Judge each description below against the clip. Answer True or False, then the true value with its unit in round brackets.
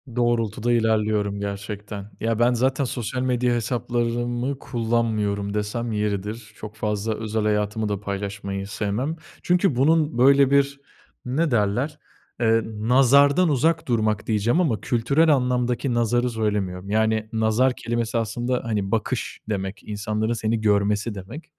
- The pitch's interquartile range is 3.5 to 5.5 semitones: False (3.0 semitones)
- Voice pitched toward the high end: False (115 Hz)